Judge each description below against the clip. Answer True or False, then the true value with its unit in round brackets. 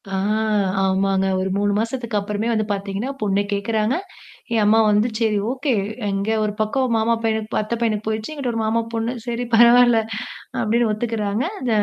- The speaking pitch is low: False (220 Hz)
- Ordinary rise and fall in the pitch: False (2.3 semitones)